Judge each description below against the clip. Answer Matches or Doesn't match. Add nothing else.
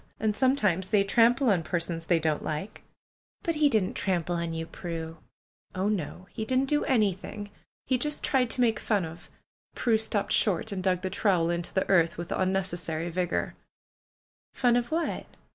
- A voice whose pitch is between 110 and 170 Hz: Doesn't match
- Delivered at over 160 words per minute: Matches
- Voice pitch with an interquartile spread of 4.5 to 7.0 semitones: Matches